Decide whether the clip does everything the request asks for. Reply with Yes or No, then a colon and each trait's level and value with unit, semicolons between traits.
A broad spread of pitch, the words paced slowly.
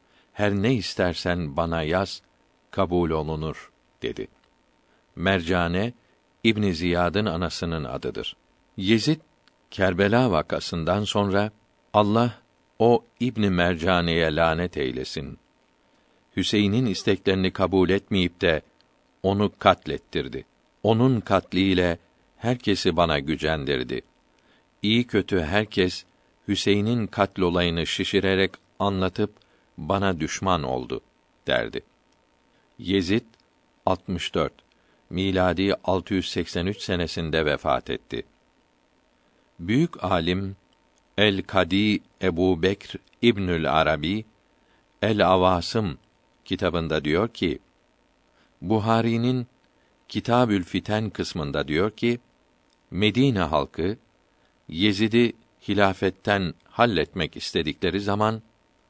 No: average, 3.0 semitones; slow, 80 wpm